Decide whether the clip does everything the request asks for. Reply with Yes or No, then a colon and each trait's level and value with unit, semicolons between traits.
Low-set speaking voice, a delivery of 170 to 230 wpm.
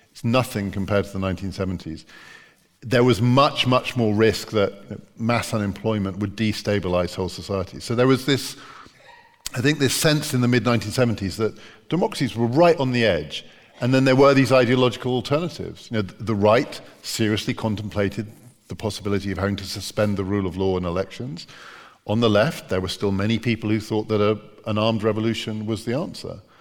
Yes: low, 110 Hz; average, 180 wpm